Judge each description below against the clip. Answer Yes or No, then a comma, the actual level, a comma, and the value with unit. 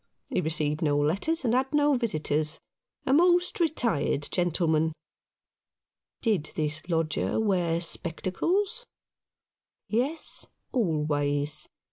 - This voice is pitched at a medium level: Yes, medium, 175 Hz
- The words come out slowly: Yes, slow, 105 wpm